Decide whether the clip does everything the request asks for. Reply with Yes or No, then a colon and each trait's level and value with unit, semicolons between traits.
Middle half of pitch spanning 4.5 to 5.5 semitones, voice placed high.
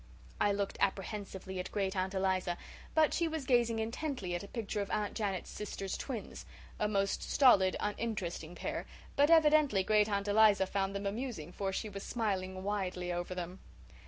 No: average, 2.9 semitones; high, 200 Hz